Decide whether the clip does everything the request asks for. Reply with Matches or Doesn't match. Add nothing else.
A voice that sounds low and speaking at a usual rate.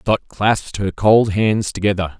Matches